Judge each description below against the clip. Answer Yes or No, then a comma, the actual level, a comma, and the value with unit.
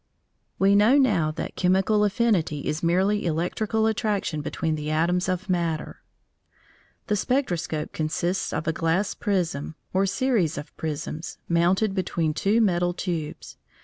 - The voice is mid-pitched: Yes, medium, 180 Hz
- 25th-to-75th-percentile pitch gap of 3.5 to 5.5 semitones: Yes, average, 4.2 semitones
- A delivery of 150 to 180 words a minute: No, slow, 135 wpm